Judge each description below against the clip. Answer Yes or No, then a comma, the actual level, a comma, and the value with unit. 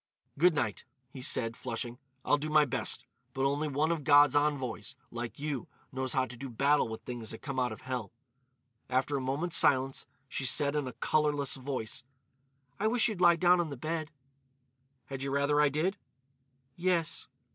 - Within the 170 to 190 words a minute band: Yes, average, 180 wpm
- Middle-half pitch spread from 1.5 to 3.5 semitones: Yes, average, 2.9 semitones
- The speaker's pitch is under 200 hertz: Yes, medium, 140 Hz